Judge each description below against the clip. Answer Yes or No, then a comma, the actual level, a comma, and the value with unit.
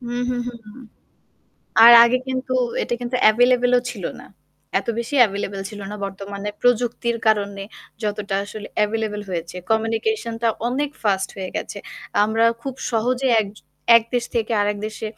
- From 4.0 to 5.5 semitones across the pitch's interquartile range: No, average, 3.0 semitones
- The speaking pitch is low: No, high, 225 Hz